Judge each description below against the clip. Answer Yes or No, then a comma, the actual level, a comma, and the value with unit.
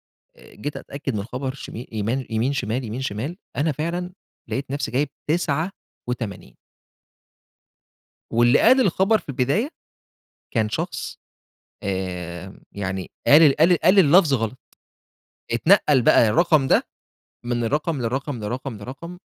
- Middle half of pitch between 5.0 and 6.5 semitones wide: Yes, wide, 5.6 semitones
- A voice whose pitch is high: No, low, 135 Hz